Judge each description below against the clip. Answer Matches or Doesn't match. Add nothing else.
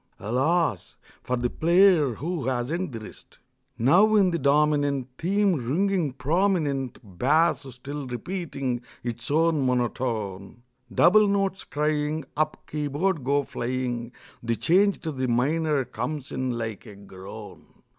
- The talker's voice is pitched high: Doesn't match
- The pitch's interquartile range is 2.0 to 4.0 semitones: Doesn't match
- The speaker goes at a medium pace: Doesn't match